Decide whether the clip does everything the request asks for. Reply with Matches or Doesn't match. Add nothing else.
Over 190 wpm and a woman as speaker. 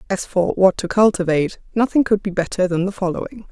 Matches